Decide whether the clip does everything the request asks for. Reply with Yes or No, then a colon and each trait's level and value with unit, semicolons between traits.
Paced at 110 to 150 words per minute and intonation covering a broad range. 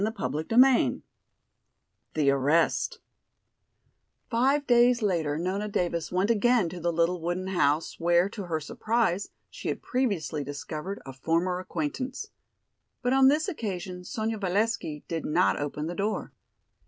Yes: slow, 135 wpm; wide, 5.8 semitones